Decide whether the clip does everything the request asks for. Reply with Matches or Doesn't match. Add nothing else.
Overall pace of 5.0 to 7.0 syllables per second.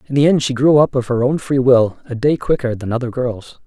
Matches